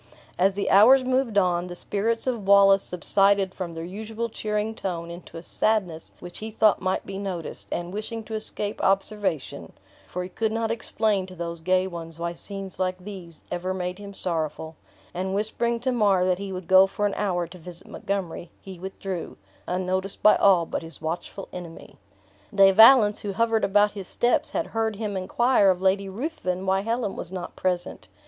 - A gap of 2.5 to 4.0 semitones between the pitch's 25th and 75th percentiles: Yes, average, 2.8 semitones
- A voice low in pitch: No, high, 195 Hz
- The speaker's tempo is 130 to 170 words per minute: No, average, 185 wpm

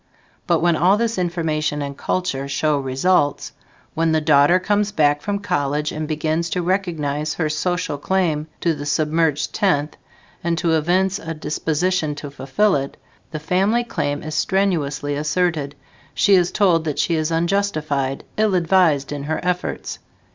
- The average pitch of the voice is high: No, medium, 160 Hz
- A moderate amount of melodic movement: Yes, average, 3.6 semitones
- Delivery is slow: No, average, 155 wpm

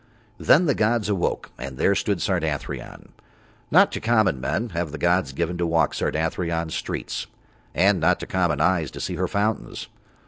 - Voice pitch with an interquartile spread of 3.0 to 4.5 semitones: Yes, average, 4.1 semitones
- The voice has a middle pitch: No, very low, 85 Hz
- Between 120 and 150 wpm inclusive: No, average, 170 wpm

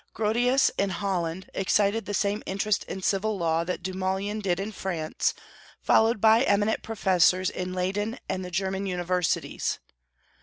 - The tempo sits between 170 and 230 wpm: No, average, 145 wpm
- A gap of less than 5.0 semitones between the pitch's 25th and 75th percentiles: Yes, narrow, 2.4 semitones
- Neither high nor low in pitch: No, high, 195 Hz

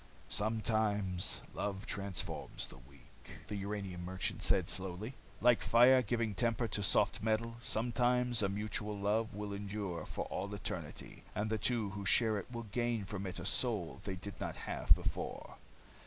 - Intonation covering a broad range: No, average, 2.7 semitones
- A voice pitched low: Yes, low, 105 Hz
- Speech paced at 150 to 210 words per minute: Yes, average, 160 wpm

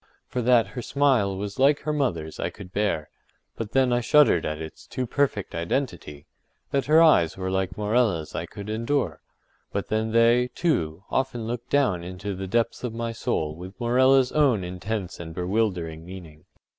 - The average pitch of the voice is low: Yes, low, 110 Hz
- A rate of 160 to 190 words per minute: Yes, average, 170 wpm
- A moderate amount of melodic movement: No, wide, 5.8 semitones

